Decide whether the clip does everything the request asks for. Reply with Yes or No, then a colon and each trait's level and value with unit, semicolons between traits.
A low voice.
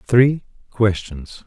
Yes: low, 110 Hz